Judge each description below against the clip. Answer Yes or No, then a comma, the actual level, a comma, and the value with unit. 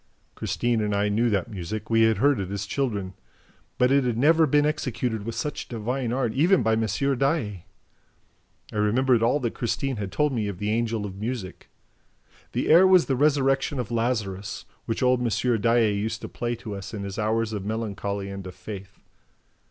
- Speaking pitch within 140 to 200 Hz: No, low, 115 Hz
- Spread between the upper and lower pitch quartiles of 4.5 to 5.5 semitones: No, average, 3.7 semitones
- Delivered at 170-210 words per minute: Yes, average, 190 wpm